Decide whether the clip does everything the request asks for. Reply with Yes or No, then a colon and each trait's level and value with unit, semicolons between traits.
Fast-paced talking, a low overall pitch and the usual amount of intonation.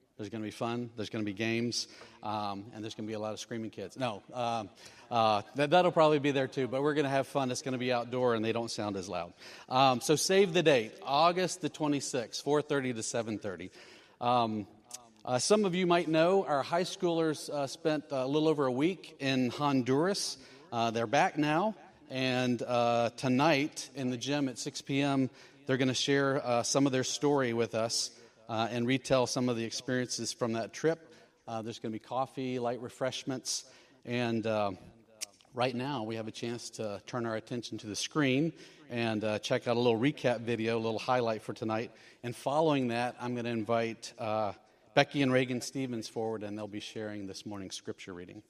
Yes: fast, 210 wpm; low, 125 Hz; average, 3.8 semitones